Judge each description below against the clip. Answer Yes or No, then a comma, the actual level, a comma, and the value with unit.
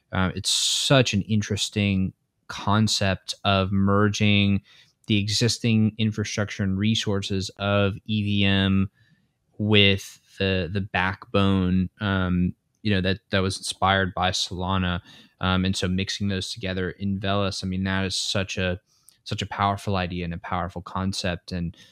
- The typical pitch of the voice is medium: No, low, 100 Hz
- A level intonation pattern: Yes, narrow, 2.0 semitones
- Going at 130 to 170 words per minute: Yes, average, 140 wpm